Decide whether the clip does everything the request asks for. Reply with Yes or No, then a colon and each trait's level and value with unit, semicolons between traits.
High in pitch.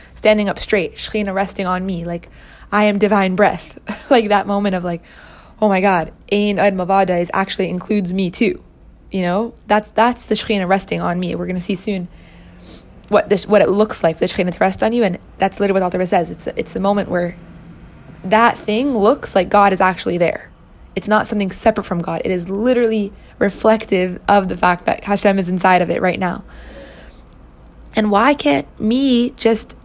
Yes: high, 200 Hz